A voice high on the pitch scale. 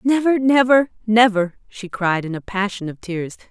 Yes: high, 215 Hz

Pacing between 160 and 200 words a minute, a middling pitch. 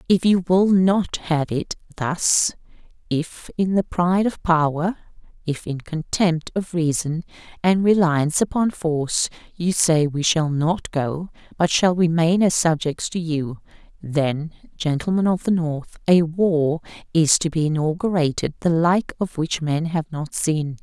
No: average, 150 wpm; medium, 165 Hz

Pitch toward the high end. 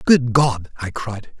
No: low, 120 Hz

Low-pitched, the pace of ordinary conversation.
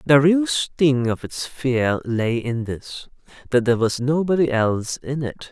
Yes: low, 130 Hz; average, 165 wpm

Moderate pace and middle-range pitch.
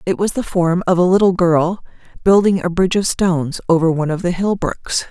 No: fast, 225 wpm; medium, 180 Hz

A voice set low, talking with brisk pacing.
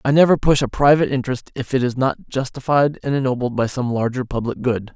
Yes: low, 130 Hz; fast, 220 wpm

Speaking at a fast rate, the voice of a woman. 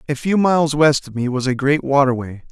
No: fast, 240 wpm; male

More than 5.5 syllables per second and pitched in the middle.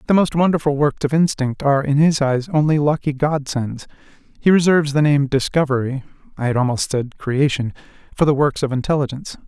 Yes: 5.9 syllables/s; medium, 145 Hz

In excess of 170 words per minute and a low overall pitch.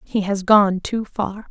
No: average, 200 wpm; high, 200 Hz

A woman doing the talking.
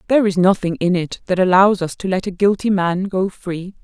Yes: female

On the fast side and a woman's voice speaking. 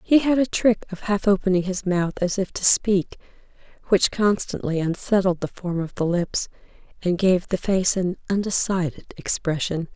No: average, 170 wpm; female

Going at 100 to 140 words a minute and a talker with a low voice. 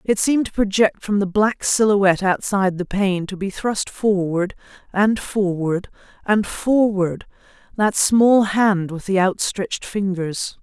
No: slow, 135 wpm; high, 200 Hz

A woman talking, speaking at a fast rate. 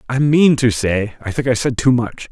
No: male; fast, 260 wpm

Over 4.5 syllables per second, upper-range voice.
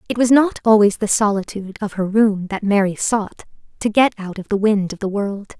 Yes: 5.3 syllables/s; high, 205 Hz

